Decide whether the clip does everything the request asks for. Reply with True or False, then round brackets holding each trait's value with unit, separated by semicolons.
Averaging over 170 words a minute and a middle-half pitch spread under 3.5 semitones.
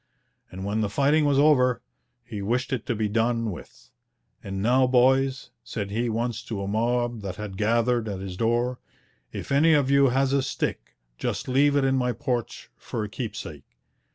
False (185 wpm; 3.8 semitones)